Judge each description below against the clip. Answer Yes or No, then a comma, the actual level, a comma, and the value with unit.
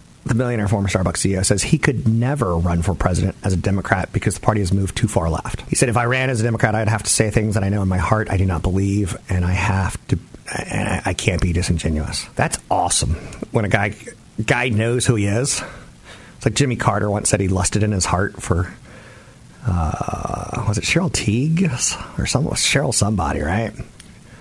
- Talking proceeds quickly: Yes, fast, 215 wpm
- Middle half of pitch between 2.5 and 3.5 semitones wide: No, average, 4.1 semitones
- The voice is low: Yes, low, 105 Hz